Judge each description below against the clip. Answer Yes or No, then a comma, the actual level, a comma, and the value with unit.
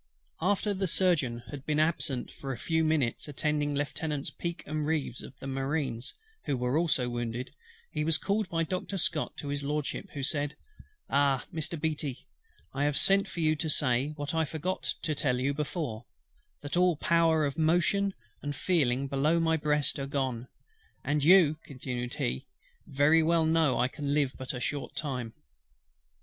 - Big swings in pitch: No, average, 3.2 semitones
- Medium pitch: Yes, medium, 145 Hz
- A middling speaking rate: Yes, average, 170 wpm